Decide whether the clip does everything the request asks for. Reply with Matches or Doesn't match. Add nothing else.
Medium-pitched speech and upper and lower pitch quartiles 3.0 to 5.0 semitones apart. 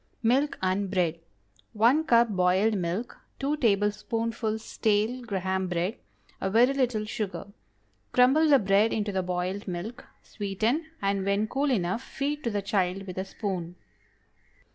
Doesn't match